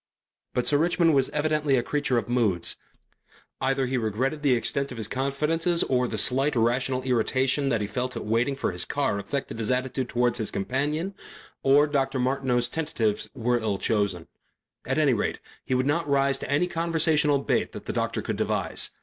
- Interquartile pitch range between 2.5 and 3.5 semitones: Yes, average, 3.2 semitones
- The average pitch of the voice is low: Yes, low, 130 Hz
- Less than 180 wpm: No, average, 185 wpm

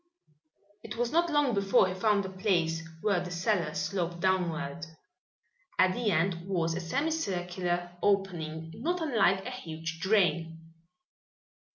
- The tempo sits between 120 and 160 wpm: Yes, average, 140 wpm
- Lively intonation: No, average, 3.8 semitones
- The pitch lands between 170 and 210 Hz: Yes, medium, 185 Hz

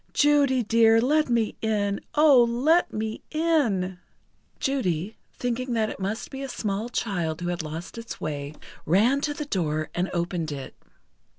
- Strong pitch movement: Yes, wide, 6.7 semitones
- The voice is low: No, high, 220 Hz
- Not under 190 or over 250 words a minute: No, average, 160 wpm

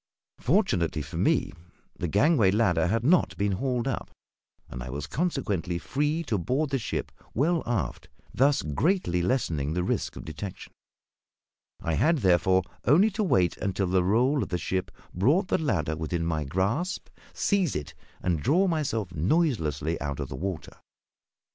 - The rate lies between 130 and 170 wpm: Yes, average, 160 wpm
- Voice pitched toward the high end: No, low, 100 Hz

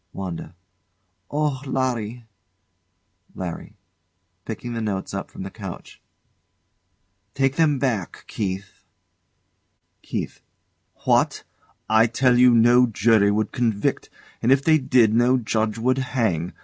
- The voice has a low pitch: Yes, low, 115 Hz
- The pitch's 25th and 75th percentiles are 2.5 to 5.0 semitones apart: Yes, average, 4.0 semitones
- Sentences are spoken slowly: Yes, slow, 115 wpm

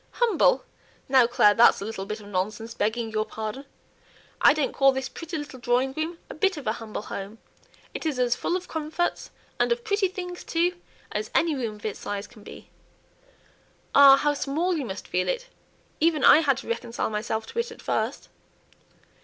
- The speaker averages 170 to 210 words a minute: Yes, average, 190 wpm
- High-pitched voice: Yes, very high, 265 Hz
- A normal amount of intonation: No, wide, 7.0 semitones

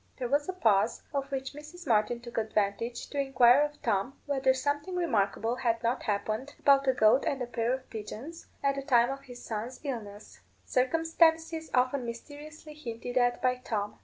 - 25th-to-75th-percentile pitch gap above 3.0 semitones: Yes, average, 3.8 semitones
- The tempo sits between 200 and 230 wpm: No, average, 180 wpm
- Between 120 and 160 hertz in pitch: No, very high, 255 Hz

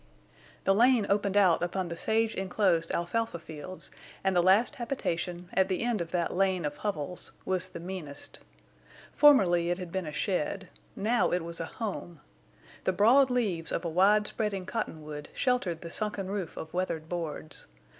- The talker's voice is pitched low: No, medium, 185 Hz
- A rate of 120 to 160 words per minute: No, average, 170 wpm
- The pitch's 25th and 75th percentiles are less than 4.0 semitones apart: Yes, average, 3.6 semitones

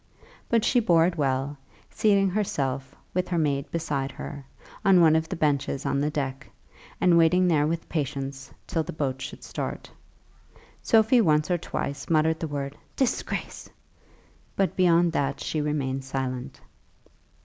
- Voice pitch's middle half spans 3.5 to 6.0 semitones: Yes, average, 4.0 semitones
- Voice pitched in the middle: Yes, medium, 155 Hz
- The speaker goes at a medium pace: Yes, average, 150 wpm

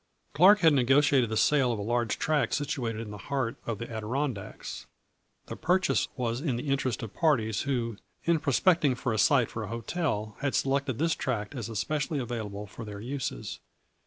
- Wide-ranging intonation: No, average, 4.4 semitones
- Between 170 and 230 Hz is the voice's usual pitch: No, low, 125 Hz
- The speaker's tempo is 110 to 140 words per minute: No, average, 190 wpm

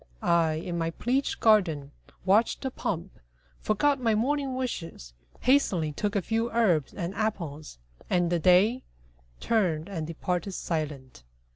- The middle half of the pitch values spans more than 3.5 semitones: Yes, wide, 5.6 semitones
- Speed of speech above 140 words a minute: No, slow, 135 wpm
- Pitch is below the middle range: No, medium, 185 Hz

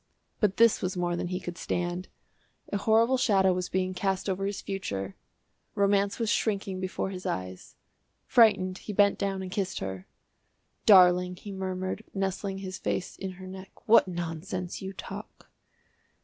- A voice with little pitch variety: Yes, narrow, 1.7 semitones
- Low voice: No, high, 190 Hz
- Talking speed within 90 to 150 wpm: No, average, 160 wpm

